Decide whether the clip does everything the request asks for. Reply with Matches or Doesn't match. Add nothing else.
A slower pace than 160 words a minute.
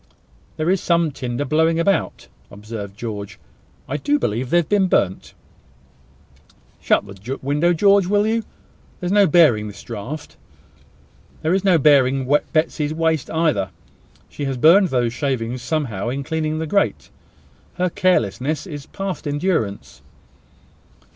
Matches